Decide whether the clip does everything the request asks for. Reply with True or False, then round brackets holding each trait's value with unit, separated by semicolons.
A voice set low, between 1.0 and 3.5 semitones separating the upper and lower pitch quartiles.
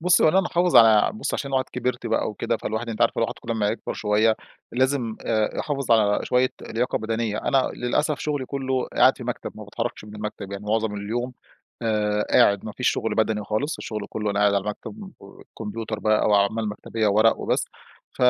True (110 Hz; 3.2 semitones)